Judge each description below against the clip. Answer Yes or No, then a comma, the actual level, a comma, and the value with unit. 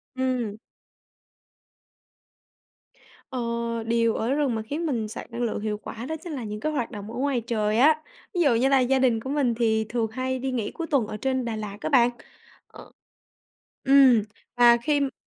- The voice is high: Yes, high, 245 Hz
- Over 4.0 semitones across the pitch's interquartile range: No, average, 3.3 semitones